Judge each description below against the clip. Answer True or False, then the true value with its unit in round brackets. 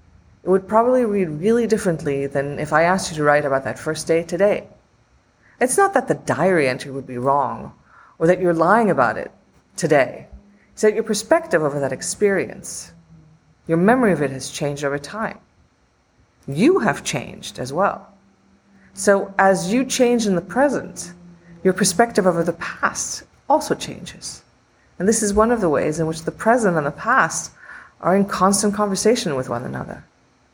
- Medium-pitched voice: True (175 Hz)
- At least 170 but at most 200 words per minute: True (175 wpm)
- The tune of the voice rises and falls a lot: True (6.5 semitones)